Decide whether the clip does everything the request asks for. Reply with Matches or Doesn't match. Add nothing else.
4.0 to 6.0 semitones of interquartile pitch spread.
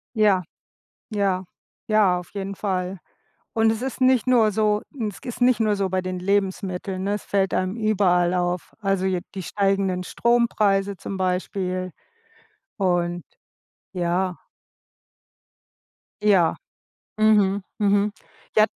Doesn't match